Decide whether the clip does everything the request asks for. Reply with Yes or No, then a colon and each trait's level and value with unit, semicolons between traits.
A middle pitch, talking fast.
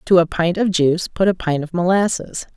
Yes: medium, 175 Hz; fast, 235 wpm